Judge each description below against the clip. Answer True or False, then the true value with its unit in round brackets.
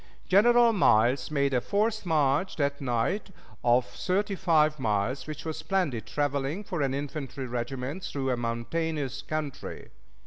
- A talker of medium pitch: True (145 Hz)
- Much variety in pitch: False (4.7 semitones)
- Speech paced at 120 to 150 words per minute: True (140 wpm)